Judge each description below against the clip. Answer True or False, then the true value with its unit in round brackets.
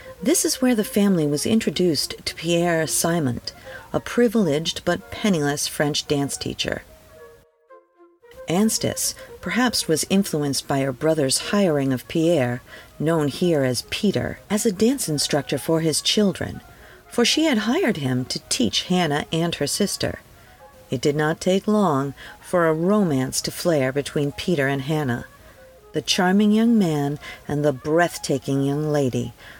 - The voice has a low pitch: False (160 Hz)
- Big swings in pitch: True (6.6 semitones)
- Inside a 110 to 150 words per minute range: True (145 wpm)